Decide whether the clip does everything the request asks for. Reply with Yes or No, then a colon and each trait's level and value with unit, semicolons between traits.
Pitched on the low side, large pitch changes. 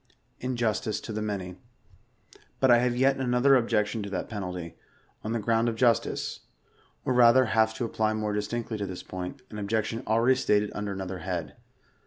No: low, 110 Hz; average, 2.7 semitones